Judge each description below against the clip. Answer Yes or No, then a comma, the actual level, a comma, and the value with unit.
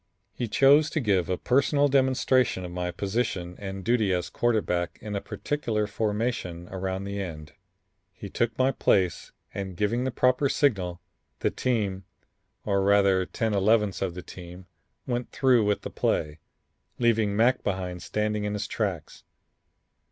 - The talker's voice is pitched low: Yes, low, 105 Hz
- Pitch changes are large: No, average, 4.3 semitones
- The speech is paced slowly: No, average, 150 wpm